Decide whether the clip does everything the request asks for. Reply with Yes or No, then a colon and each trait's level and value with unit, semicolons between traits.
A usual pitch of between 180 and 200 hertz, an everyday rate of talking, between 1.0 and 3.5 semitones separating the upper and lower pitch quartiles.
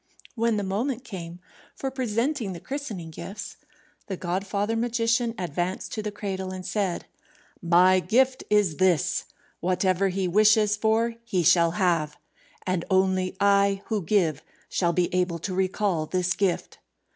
Yes: high, 190 Hz; average, 145 wpm; average, 3.1 semitones